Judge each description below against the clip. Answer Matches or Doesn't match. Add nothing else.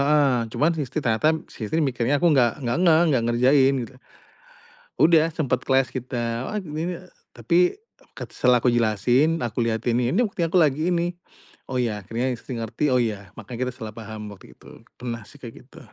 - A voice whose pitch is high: Doesn't match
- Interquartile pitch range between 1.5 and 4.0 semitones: Doesn't match